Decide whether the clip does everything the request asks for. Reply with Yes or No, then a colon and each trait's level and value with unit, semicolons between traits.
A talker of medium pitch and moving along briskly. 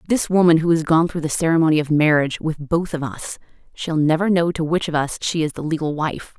Yes: medium, 160 Hz; fast, 245 wpm